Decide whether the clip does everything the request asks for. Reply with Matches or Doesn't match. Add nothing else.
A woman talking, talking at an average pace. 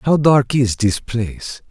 Doesn't match